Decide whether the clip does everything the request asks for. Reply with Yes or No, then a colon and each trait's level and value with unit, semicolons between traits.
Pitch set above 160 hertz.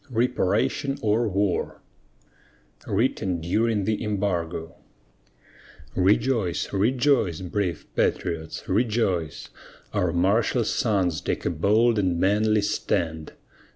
No: low, 100 Hz